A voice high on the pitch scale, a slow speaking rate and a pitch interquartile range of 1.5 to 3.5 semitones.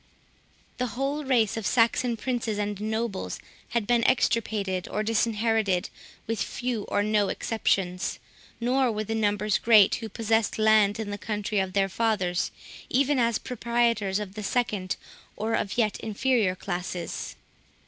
No: high, 220 Hz; average, 145 wpm; narrow, 2.4 semitones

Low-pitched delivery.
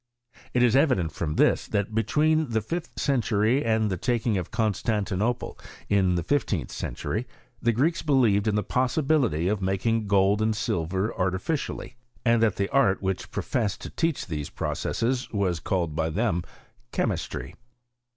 Yes: low, 110 Hz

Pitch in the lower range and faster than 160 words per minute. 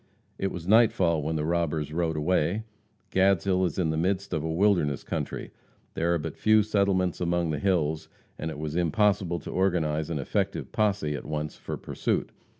Yes: very low, 85 Hz; average, 180 wpm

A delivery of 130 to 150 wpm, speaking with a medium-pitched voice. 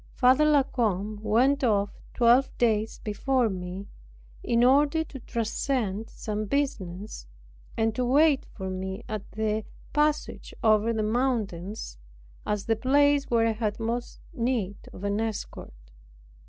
No: slow, 135 wpm; high, 225 Hz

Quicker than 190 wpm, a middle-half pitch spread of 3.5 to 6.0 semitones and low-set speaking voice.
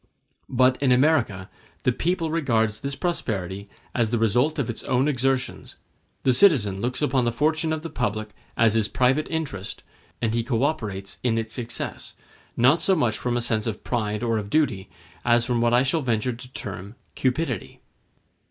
No: average, 180 wpm; average, 3.9 semitones; low, 120 Hz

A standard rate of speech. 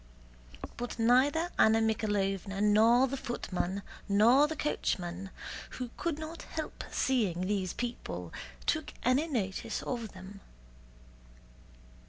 No: slow, 110 wpm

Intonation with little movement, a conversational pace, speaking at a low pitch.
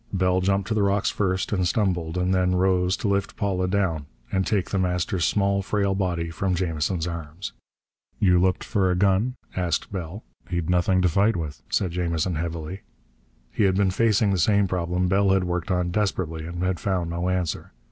Yes: narrow, 2.0 semitones; average, 190 wpm; very low, 90 Hz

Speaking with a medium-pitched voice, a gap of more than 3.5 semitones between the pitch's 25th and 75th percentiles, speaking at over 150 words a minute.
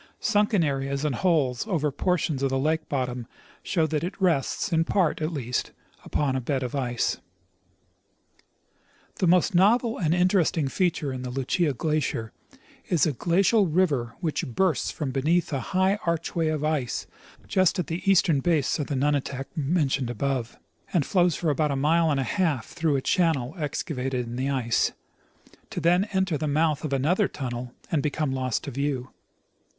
Yes: medium, 150 Hz; average, 4.6 semitones; average, 170 wpm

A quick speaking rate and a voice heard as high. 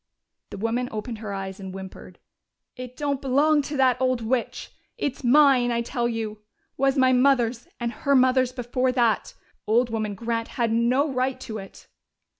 No: average, 170 wpm; high, 245 Hz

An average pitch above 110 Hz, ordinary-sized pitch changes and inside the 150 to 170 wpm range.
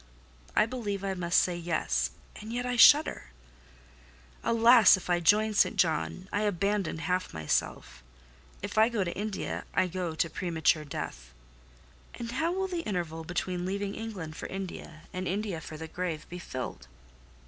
Yes: medium, 185 Hz; average, 4.7 semitones; average, 160 wpm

